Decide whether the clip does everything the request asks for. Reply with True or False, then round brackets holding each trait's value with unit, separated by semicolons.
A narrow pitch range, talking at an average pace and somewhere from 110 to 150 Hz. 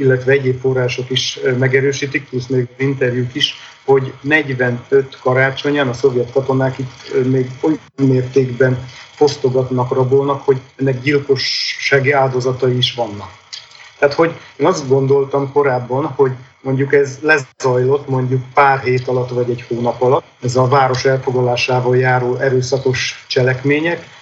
True (1.4 semitones; 130 wpm; 130 Hz)